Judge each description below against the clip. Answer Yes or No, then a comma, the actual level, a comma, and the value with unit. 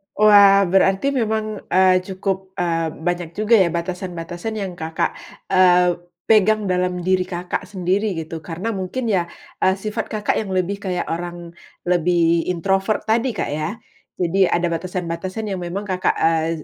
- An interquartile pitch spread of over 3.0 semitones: No, narrow, 2.6 semitones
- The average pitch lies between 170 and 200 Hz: Yes, medium, 185 Hz